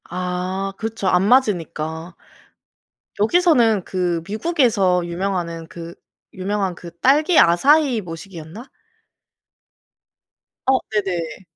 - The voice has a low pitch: No, high, 190 Hz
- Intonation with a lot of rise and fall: No, average, 4.7 semitones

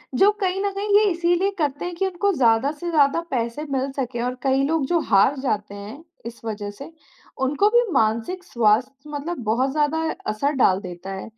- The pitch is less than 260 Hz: No, very high, 275 Hz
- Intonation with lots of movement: Yes, wide, 6.9 semitones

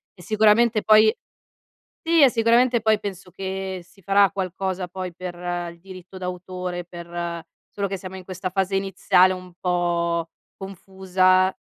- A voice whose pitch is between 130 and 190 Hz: Yes, medium, 185 Hz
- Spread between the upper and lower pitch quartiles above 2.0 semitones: No, narrow, 1.7 semitones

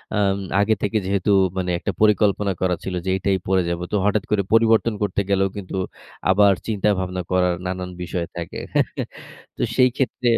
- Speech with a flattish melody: Yes, narrow, 2.2 semitones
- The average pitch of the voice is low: Yes, low, 100 Hz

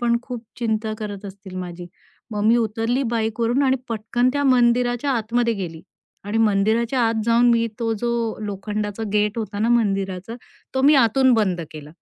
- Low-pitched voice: No, high, 225 Hz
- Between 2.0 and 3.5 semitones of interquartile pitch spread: Yes, average, 2.7 semitones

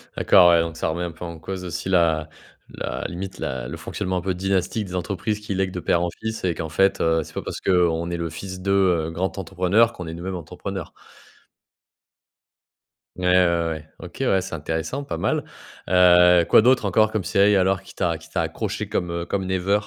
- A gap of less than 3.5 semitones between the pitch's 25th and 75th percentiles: Yes, narrow, 2.4 semitones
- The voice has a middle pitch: No, very low, 90 Hz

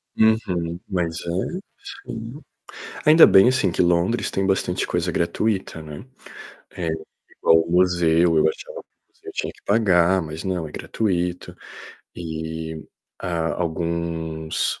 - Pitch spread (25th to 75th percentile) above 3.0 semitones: No, average, 2.7 semitones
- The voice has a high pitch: No, very low, 85 Hz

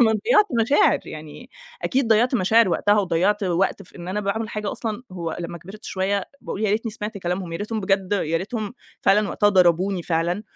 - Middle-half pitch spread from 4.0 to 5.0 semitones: No, average, 3.3 semitones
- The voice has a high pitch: Yes, high, 200 Hz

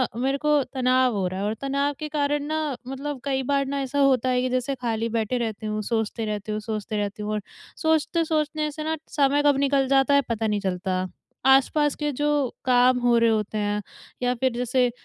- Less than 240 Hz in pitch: No, very high, 255 Hz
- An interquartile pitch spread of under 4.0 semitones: No, average, 4.4 semitones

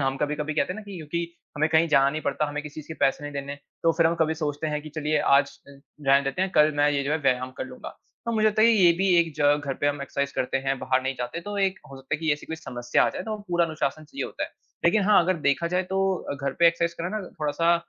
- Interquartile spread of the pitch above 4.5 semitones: No, average, 3.4 semitones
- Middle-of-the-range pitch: Yes, medium, 155 Hz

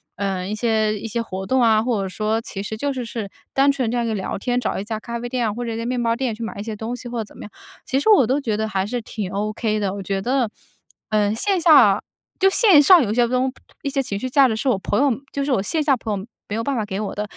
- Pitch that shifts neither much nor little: Yes, average, 3.5 semitones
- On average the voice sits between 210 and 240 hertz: Yes, high, 230 Hz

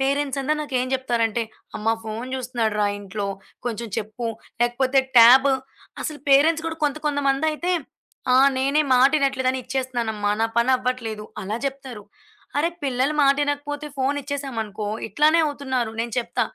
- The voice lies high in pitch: Yes, very high, 260 Hz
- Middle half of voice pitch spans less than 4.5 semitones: Yes, average, 3.4 semitones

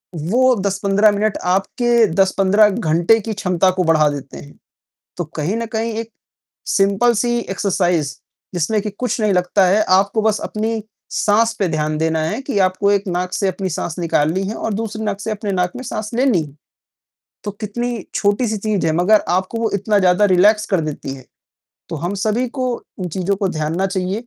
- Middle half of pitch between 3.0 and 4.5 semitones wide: Yes, average, 3.4 semitones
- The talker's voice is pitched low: No, high, 200 Hz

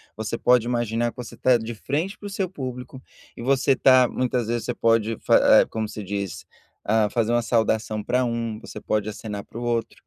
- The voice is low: Yes, low, 115 Hz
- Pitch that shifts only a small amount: Yes, narrow, 2.3 semitones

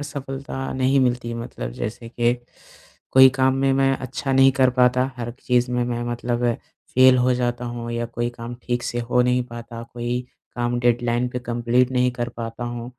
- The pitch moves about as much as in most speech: No, narrow, 1.2 semitones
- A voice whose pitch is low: Yes, low, 120 Hz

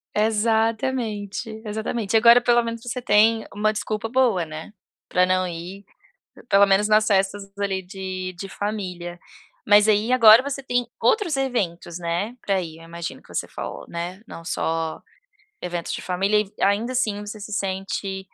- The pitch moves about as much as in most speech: Yes, average, 3.3 semitones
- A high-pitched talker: Yes, high, 205 Hz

